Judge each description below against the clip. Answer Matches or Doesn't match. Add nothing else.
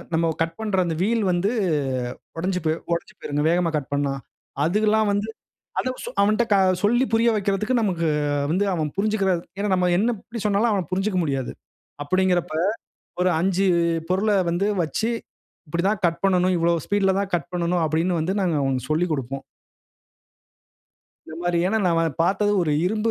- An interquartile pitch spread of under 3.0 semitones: Doesn't match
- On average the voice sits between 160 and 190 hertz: Matches